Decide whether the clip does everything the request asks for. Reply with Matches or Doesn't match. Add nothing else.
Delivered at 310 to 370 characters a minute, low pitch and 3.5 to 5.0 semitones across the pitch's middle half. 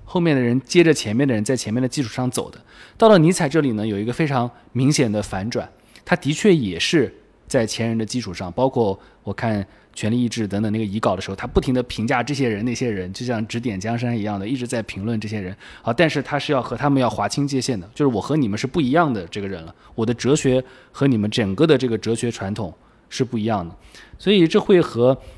Matches